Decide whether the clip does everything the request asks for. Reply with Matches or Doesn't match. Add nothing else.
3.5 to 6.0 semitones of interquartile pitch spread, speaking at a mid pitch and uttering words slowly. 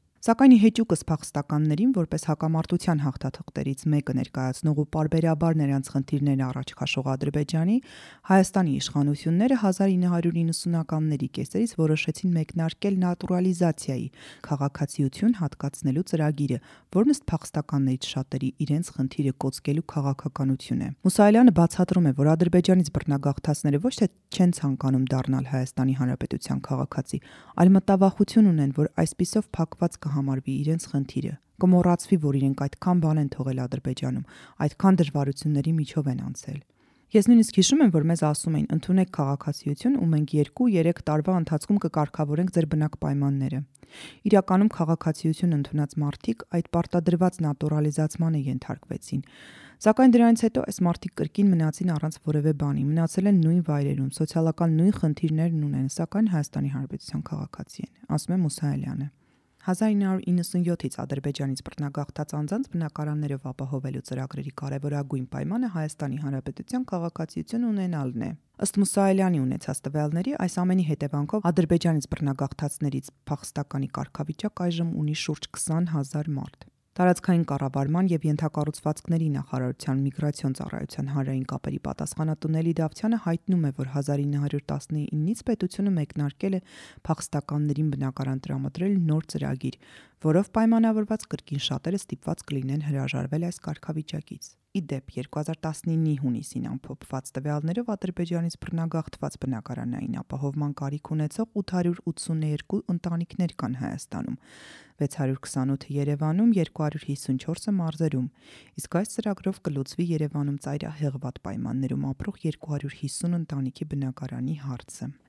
Matches